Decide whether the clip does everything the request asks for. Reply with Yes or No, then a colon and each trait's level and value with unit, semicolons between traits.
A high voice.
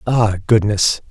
No: low, 105 Hz